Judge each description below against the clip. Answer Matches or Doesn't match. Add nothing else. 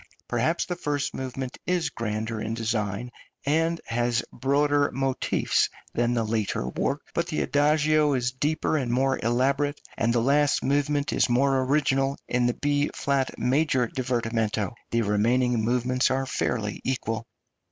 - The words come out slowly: Doesn't match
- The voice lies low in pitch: Matches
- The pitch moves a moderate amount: Matches